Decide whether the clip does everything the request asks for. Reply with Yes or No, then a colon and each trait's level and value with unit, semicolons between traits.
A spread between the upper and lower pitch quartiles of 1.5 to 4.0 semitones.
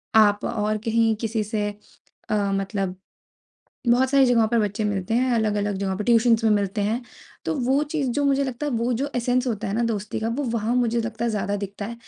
Yes: average, 2.8 semitones